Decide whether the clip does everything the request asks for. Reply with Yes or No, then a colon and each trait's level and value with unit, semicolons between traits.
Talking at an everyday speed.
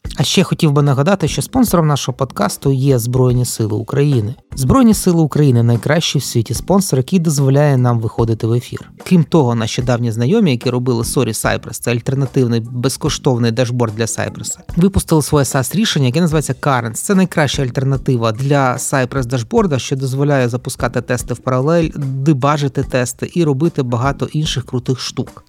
No: fast, 160 wpm